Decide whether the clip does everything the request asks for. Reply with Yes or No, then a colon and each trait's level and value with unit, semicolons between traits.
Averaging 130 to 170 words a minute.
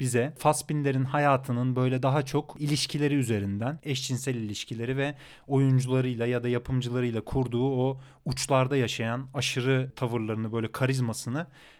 No: average, 115 wpm